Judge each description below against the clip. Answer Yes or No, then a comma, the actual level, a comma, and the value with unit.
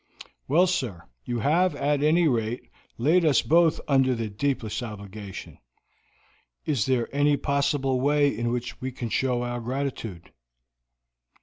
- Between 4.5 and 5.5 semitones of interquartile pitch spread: No, average, 3.7 semitones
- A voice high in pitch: No, low, 130 Hz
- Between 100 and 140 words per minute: Yes, slow, 135 wpm